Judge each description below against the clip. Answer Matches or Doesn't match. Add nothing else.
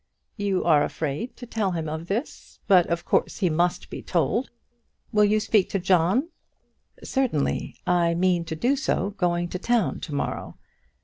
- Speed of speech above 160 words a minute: Matches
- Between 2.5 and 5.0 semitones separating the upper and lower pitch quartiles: Matches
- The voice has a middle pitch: Matches